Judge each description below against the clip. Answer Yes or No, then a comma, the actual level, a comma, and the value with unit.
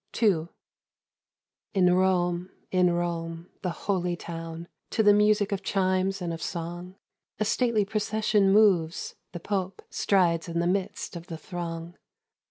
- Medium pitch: Yes, medium, 180 Hz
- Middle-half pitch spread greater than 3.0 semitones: No, narrow, 2.6 semitones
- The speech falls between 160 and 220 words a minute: No, average, 145 wpm